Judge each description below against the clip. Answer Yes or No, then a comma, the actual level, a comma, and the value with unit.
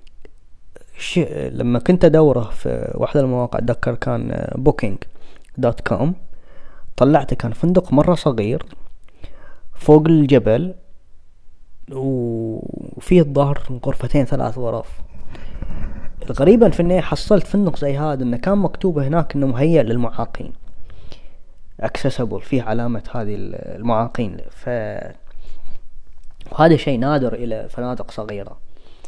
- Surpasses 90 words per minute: Yes, average, 105 wpm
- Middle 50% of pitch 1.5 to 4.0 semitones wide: No, average, 5.1 semitones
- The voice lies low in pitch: Yes, low, 130 Hz